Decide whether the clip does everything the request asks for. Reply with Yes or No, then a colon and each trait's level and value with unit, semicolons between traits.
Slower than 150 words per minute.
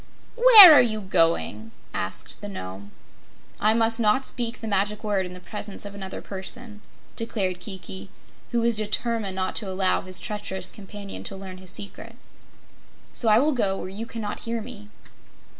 No: average, 170 wpm